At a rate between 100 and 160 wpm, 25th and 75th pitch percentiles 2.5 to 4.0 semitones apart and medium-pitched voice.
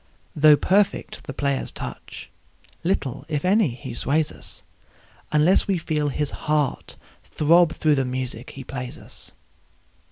Yes: slow, 135 wpm; average, 3.3 semitones; medium, 150 Hz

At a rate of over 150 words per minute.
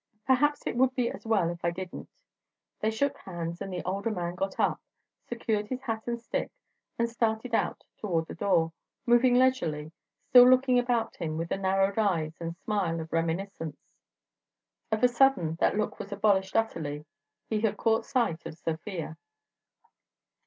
Yes: average, 165 wpm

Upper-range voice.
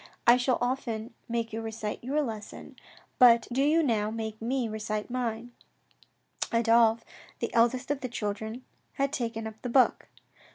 Yes: high, 235 Hz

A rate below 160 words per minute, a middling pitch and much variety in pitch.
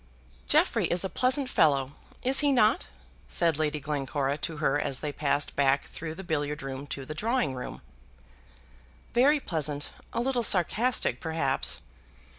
Yes: average, 150 wpm; medium, 155 Hz; wide, 7.8 semitones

